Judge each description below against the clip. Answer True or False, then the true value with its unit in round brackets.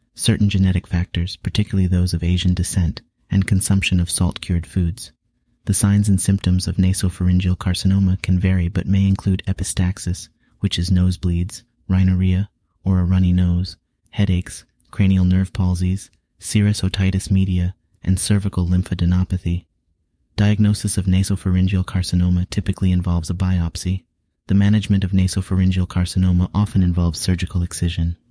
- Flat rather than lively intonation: True (1.5 semitones)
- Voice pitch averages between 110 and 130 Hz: False (95 Hz)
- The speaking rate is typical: False (130 wpm)